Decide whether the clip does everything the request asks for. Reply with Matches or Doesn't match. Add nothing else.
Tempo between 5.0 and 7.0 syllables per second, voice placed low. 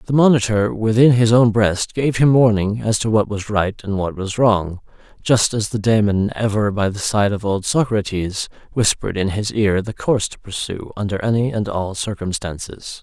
Doesn't match